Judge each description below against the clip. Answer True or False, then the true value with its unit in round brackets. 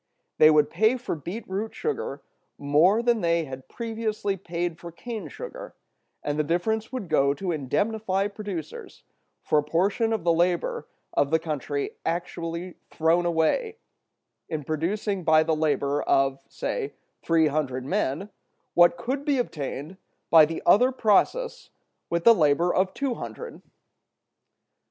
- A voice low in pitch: False (175 Hz)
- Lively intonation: True (5.7 semitones)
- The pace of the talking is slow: False (145 wpm)